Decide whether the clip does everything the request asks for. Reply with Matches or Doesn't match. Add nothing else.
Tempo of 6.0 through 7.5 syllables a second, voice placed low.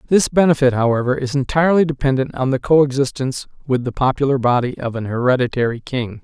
Matches